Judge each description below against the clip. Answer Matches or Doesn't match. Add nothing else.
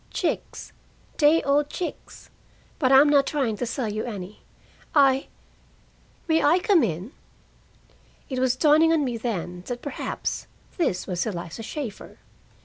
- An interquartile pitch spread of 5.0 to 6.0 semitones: Matches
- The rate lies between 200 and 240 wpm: Doesn't match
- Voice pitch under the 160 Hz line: Doesn't match